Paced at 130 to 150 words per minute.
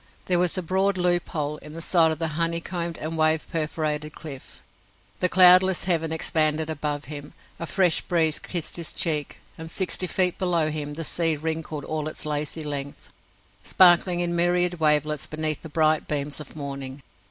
No: average, 175 wpm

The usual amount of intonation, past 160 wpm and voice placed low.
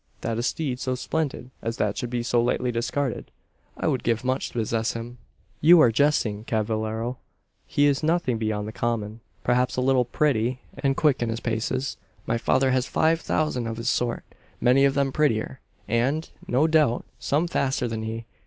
Yes: average, 3.2 semitones; average, 185 wpm; low, 125 Hz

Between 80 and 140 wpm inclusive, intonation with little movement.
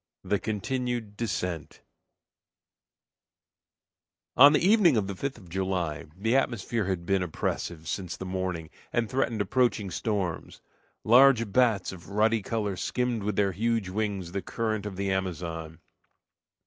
No: slow, 135 wpm; average, 3.8 semitones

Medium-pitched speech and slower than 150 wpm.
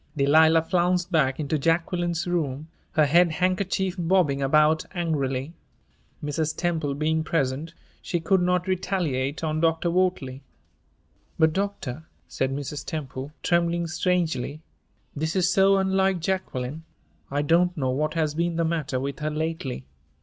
Yes: medium, 160 Hz; slow, 135 wpm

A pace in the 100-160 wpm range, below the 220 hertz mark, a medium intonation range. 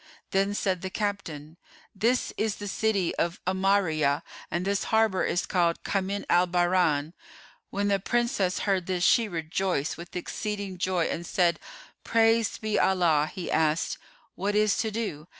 Yes: average, 150 wpm; high, 190 Hz; average, 3.0 semitones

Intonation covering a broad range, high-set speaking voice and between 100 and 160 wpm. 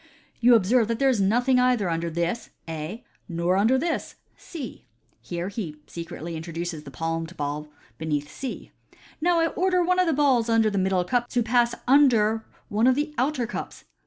No: wide, 7.0 semitones; high, 220 Hz; average, 190 wpm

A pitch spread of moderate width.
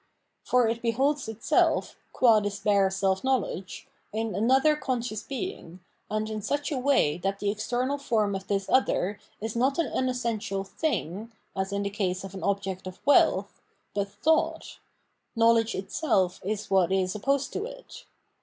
Yes: average, 4.8 semitones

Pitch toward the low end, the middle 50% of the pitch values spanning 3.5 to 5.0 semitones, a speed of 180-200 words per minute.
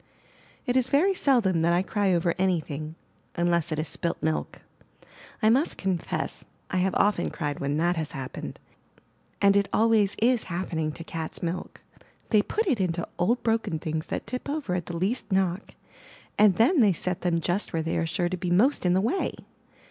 No: medium, 185 Hz; average, 4.6 semitones; average, 195 wpm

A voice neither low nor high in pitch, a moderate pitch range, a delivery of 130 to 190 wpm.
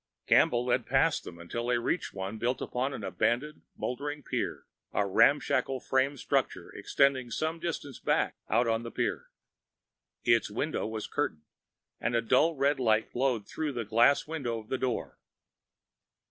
No: low, 125 Hz; average, 3.6 semitones; average, 155 wpm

